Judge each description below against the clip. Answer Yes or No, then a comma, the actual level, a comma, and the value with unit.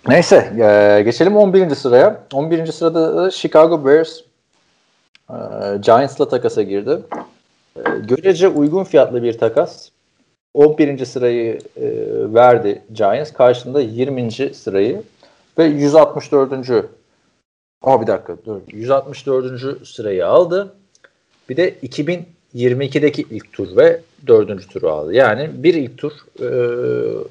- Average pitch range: No, wide, 7.0 semitones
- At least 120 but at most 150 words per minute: No, average, 100 wpm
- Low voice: No, medium, 150 Hz